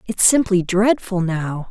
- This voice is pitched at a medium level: No, high, 195 Hz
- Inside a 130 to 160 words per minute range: Yes, average, 140 wpm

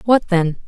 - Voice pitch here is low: No, high, 195 Hz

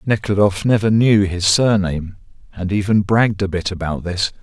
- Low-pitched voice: Yes, low, 100 Hz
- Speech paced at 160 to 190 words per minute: Yes, average, 165 wpm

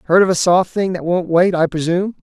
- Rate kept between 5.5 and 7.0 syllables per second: Yes, 6.0 syllables/s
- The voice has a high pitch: No, medium, 175 Hz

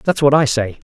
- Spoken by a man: Yes, male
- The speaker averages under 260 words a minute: No, fast, 265 wpm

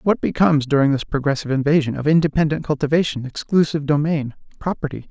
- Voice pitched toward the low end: No, medium, 150 Hz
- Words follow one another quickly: No, average, 140 wpm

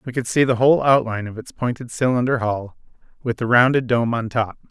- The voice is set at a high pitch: No, low, 120 Hz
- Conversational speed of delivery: No, fast, 215 wpm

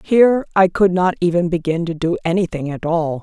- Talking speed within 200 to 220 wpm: Yes, fast, 205 wpm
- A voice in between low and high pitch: Yes, medium, 175 Hz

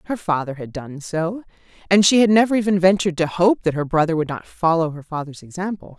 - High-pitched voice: No, medium, 175 Hz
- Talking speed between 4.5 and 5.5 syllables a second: No, 6.0 syllables/s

